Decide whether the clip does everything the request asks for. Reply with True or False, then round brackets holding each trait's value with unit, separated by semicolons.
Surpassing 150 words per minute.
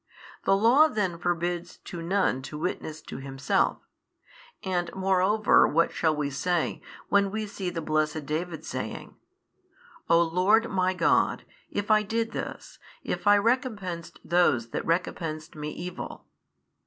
False (140 wpm)